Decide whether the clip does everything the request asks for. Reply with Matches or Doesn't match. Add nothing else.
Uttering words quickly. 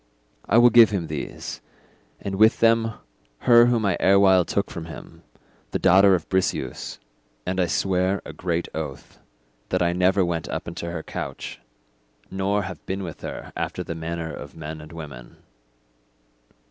Doesn't match